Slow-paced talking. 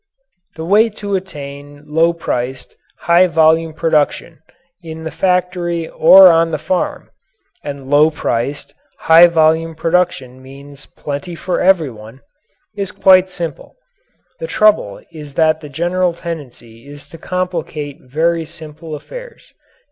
Yes: slow, 125 wpm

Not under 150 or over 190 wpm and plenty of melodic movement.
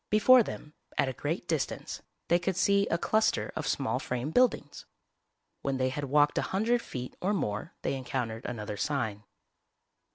Yes: average, 165 wpm; wide, 6.9 semitones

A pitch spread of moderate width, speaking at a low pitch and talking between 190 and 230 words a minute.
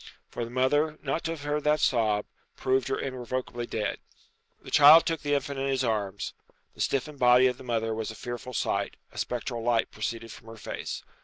Yes: average, 3.6 semitones; low, 125 Hz; fast, 205 wpm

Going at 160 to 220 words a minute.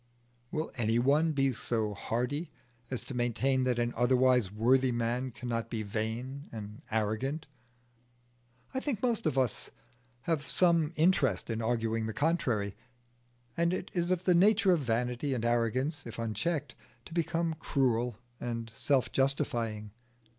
No: average, 145 wpm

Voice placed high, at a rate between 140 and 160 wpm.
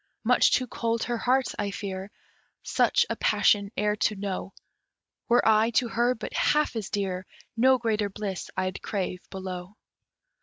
Yes: high, 210 Hz; average, 155 wpm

